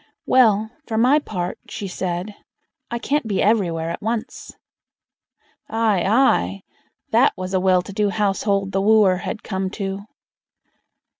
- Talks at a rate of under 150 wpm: Yes, average, 140 wpm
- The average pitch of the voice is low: No, high, 200 Hz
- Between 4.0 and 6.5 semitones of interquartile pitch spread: No, average, 2.9 semitones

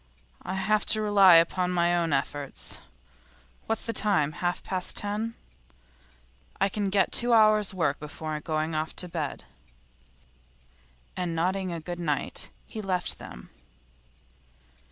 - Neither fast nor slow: No, slow, 130 wpm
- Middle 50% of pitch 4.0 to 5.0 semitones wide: Yes, average, 4.3 semitones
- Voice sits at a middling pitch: Yes, medium, 180 Hz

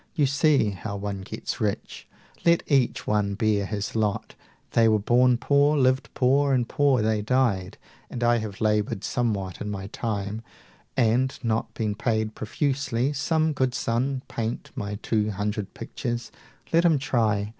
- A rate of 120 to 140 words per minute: No, average, 160 wpm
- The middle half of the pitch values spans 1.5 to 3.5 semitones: No, average, 3.9 semitones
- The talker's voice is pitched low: Yes, low, 115 Hz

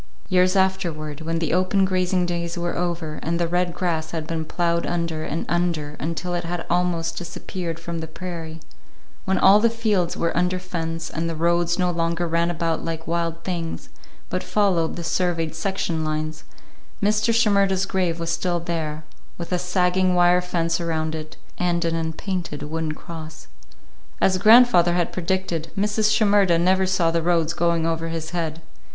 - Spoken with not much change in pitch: Yes, narrow, 1.8 semitones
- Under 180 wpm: Yes, average, 170 wpm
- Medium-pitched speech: Yes, medium, 170 Hz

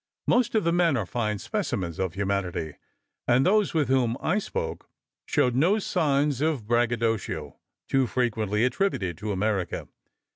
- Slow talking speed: No, average, 145 wpm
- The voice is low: Yes, low, 120 Hz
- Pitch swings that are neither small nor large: No, wide, 7.2 semitones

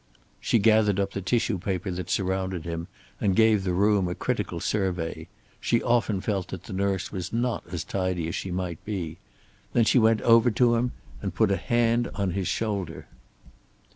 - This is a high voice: No, low, 100 Hz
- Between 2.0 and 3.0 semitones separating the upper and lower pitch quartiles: No, average, 3.4 semitones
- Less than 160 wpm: No, average, 185 wpm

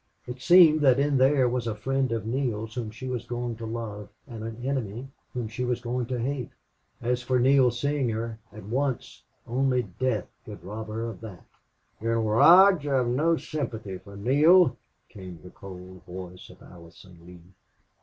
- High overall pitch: No, low, 120 Hz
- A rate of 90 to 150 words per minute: No, average, 180 wpm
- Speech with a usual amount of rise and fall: Yes, average, 3.7 semitones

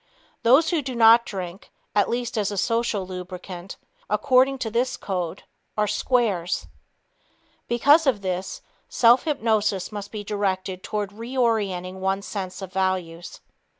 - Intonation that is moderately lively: Yes, average, 4.1 semitones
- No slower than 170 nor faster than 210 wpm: No, slow, 135 wpm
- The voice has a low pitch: No, high, 205 Hz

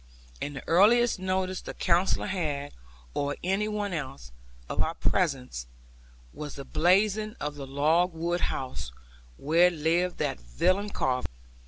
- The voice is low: No, medium, 170 Hz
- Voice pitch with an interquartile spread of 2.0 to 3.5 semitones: No, average, 4.8 semitones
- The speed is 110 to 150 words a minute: Yes, average, 140 wpm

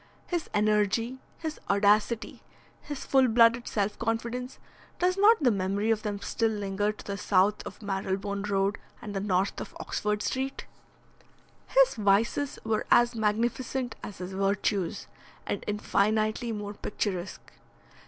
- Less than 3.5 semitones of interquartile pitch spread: Yes, average, 2.9 semitones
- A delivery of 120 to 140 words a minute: Yes, slow, 135 wpm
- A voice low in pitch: No, high, 210 Hz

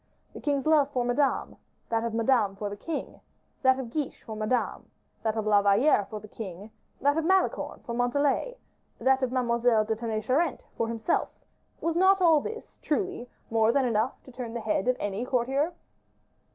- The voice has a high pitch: Yes, high, 245 Hz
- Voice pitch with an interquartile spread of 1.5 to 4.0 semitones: No, average, 4.5 semitones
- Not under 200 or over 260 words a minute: No, average, 185 wpm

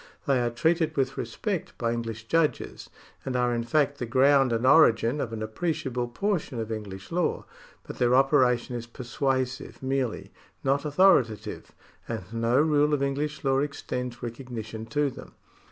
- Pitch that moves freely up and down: No, average, 3.6 semitones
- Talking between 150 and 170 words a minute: Yes, average, 160 wpm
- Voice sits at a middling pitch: No, low, 130 Hz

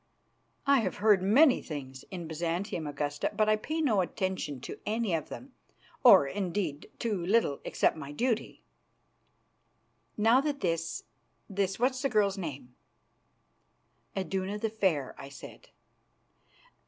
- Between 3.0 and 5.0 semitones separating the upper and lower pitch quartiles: No, wide, 5.5 semitones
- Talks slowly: Yes, slow, 130 wpm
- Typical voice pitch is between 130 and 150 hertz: No, high, 190 Hz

